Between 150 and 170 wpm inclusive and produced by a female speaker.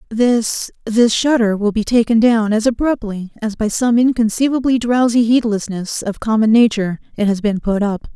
Yes: average, 160 wpm; female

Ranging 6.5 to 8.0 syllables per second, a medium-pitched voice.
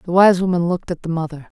Yes: 7.2 syllables/s; medium, 175 Hz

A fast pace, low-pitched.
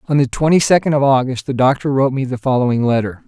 Yes: fast, 240 wpm; low, 130 Hz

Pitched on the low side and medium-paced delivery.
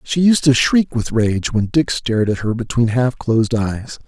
No: low, 120 Hz; fast, 220 wpm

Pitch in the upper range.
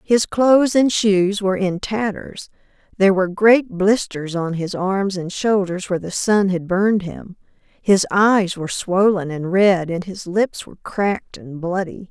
Yes: high, 195 Hz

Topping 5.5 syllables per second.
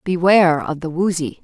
No: 5.3 syllables/s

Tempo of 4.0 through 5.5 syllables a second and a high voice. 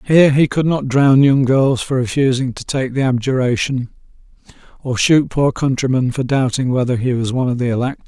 No: 5.4 syllables/s; low, 130 Hz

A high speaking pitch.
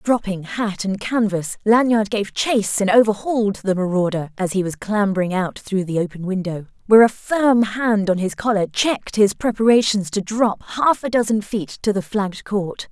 Yes: high, 205 Hz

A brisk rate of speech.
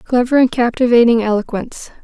No: slow, 120 wpm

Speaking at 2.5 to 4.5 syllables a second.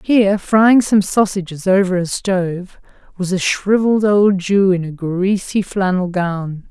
Yes: 4.2 syllables/s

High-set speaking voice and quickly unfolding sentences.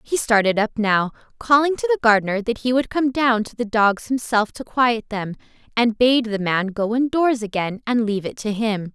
Yes: high, 230 Hz; fast, 215 wpm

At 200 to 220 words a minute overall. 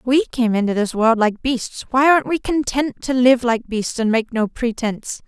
Yes: fast, 205 wpm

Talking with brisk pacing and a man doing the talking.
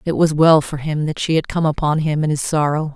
No: fast, 285 wpm; female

